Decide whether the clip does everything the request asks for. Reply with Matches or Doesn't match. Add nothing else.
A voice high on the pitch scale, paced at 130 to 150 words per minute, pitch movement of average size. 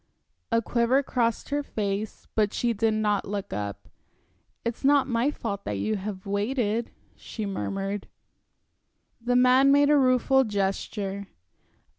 Matches